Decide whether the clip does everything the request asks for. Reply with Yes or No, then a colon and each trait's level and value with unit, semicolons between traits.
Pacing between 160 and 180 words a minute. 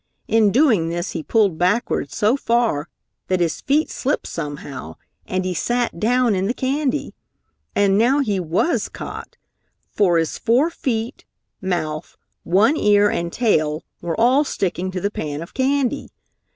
No: average, 150 wpm